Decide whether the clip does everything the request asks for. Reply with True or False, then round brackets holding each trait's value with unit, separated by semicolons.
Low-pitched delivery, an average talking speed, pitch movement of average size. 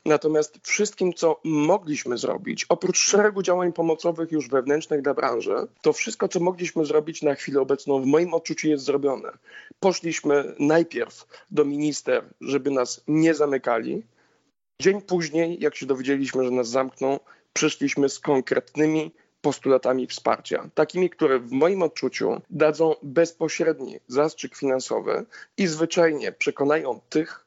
False (155 Hz; 130 wpm; 3.1 semitones)